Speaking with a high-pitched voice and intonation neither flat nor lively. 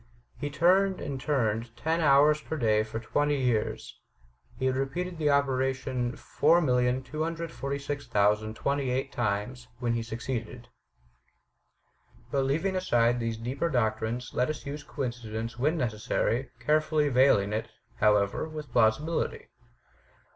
No: low, 130 Hz; average, 4.2 semitones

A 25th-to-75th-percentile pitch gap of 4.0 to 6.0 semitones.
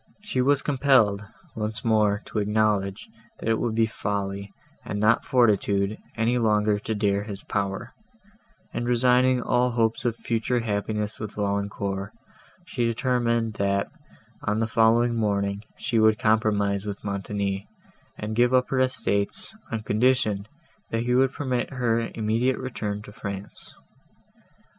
No: average, 2.9 semitones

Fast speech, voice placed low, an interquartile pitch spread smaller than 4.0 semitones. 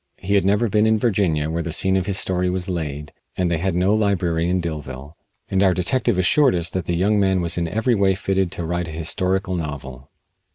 Yes: fast, 230 wpm; very low, 90 Hz; average, 2.8 semitones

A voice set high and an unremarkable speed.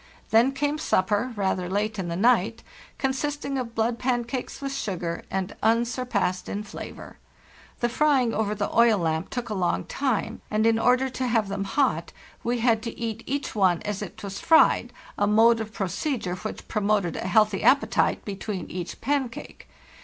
Yes: high, 225 Hz; average, 165 wpm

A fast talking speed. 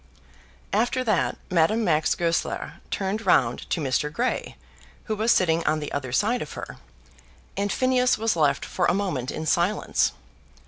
No: average, 155 wpm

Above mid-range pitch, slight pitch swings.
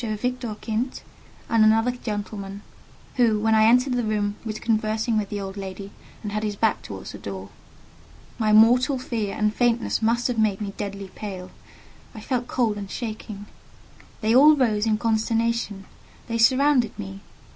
Yes: high, 220 Hz; narrow, 2.3 semitones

